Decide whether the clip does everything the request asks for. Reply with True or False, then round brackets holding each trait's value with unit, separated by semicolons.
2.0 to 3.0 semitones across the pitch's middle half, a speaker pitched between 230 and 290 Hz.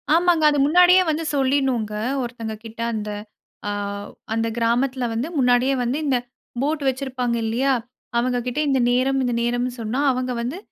True (2.5 semitones; 255 Hz)